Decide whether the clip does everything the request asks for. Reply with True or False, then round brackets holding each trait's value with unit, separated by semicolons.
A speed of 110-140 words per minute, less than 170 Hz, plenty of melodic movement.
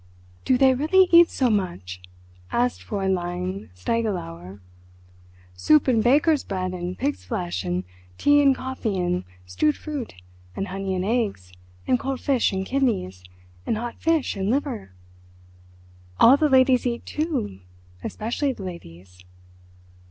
False (135 wpm; 205 Hz; 7.4 semitones)